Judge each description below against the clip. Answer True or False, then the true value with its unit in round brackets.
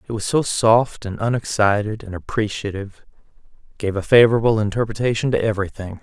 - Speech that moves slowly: True (130 wpm)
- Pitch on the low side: True (105 Hz)